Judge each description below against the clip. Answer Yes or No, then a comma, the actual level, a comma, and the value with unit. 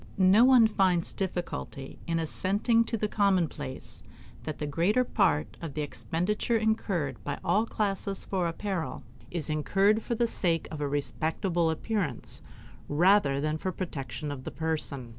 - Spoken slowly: No, average, 155 wpm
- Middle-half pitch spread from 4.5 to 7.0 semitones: Yes, average, 5.2 semitones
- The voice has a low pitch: No, medium, 175 Hz